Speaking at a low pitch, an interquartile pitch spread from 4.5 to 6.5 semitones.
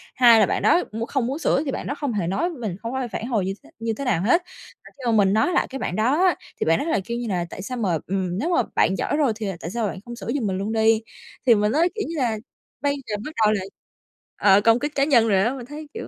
No: high, 230 Hz; average, 5.2 semitones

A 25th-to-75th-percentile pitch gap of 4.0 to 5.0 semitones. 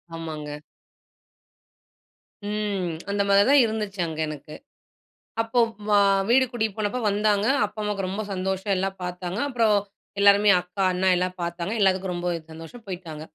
No: average, 2.9 semitones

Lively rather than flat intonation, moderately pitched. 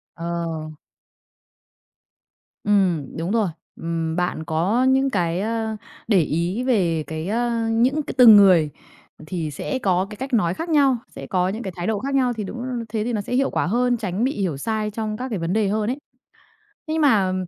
No: wide, 5.7 semitones; high, 210 Hz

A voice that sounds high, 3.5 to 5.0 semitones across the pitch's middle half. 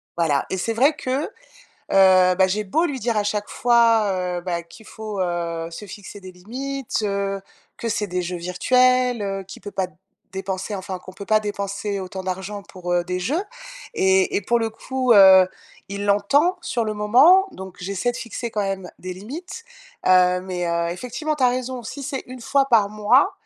Yes: high, 200 Hz; average, 4.5 semitones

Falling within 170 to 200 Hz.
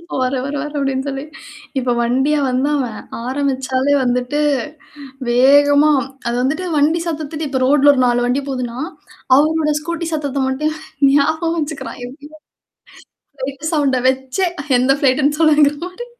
No: very high, 280 Hz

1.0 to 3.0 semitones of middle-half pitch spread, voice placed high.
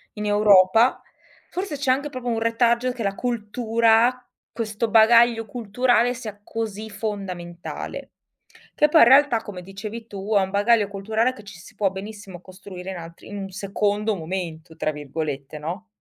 No: average, 3.4 semitones; high, 210 Hz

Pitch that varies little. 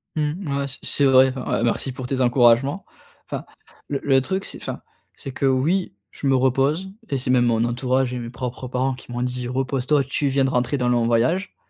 Yes: narrow, 2.0 semitones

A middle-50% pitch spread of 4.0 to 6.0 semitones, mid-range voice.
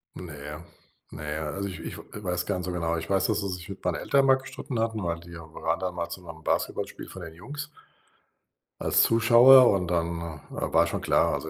No: average, 4.4 semitones; very low, 90 Hz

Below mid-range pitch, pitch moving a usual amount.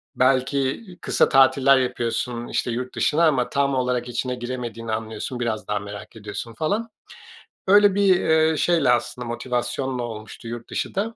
Yes: low, 125 Hz; average, 3.0 semitones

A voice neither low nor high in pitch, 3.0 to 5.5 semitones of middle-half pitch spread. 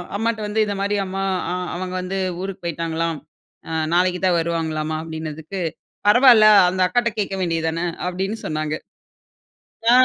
Yes: medium, 180 Hz; average, 3.6 semitones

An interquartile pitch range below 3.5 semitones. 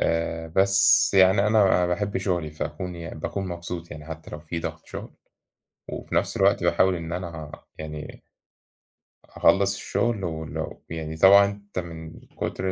Yes: average, 3.0 semitones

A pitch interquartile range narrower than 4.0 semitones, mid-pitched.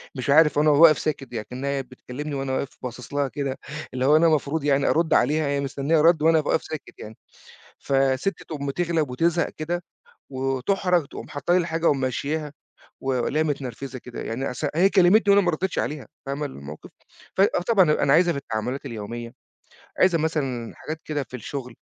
Yes: average, 3.5 semitones; medium, 145 Hz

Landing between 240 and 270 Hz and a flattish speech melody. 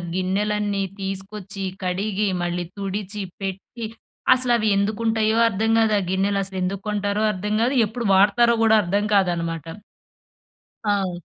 No: high, 200 Hz; narrow, 2.0 semitones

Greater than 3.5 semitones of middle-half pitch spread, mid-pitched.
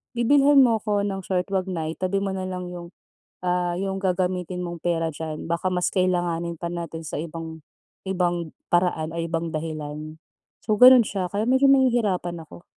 No: average, 2.8 semitones; medium, 180 Hz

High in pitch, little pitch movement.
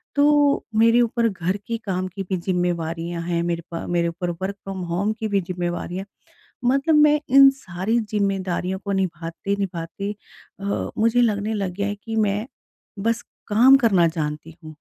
No: high, 195 Hz; average, 4.2 semitones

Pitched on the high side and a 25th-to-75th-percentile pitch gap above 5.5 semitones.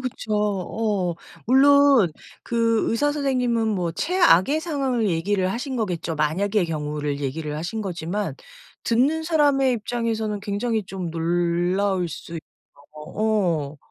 Yes: high, 205 Hz; wide, 6.1 semitones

